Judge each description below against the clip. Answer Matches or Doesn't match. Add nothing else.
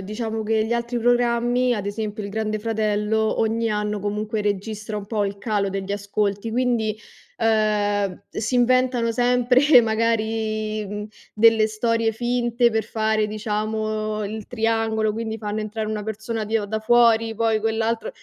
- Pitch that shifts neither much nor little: Doesn't match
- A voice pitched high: Matches